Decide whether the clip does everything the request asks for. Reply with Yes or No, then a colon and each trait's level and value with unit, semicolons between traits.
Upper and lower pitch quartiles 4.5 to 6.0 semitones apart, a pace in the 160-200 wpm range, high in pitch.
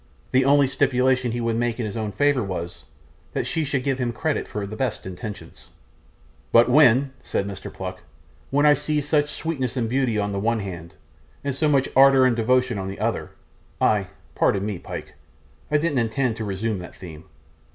No: average, 4.9 semitones; average, 195 wpm; low, 120 Hz